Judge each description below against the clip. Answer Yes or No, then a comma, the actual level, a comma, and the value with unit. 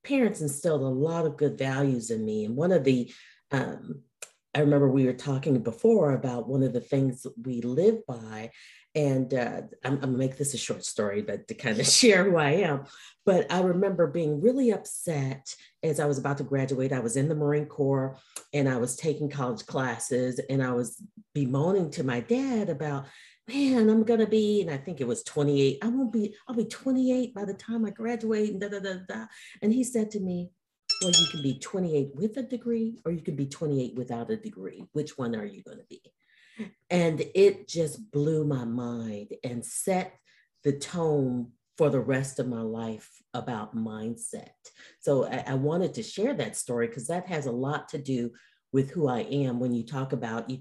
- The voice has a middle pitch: Yes, medium, 145 Hz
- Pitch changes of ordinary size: No, wide, 7.3 semitones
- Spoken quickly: Yes, fast, 210 wpm